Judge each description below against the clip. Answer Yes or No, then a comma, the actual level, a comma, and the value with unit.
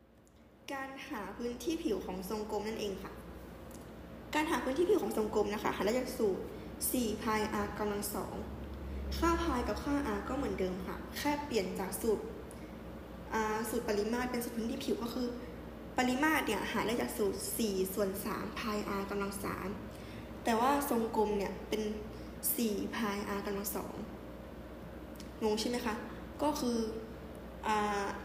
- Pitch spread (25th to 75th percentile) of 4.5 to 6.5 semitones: No, average, 3.6 semitones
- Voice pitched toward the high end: Yes, high, 220 Hz